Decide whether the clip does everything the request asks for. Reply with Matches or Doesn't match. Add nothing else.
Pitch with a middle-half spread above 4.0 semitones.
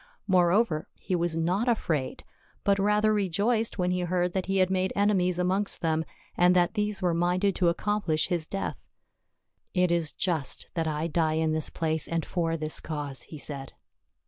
Doesn't match